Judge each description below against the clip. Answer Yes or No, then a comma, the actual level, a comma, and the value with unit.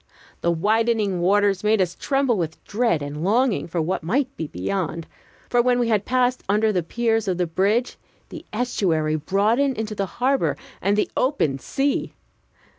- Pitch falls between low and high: No, high, 210 Hz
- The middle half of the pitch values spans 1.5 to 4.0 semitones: No, wide, 5.5 semitones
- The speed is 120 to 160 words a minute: No, average, 170 wpm